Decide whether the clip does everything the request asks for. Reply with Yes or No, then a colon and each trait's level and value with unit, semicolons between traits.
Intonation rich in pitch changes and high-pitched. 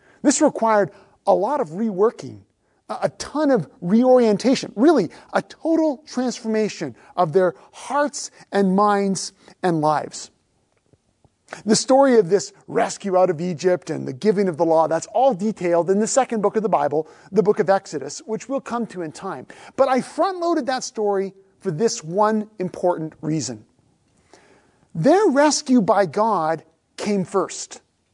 Yes: wide, 5.7 semitones; high, 205 Hz